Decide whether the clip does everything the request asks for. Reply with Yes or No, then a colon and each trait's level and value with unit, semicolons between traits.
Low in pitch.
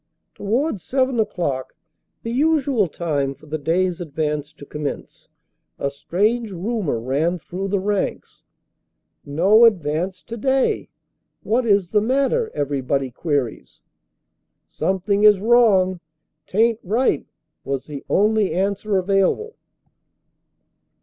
No: high, 190 Hz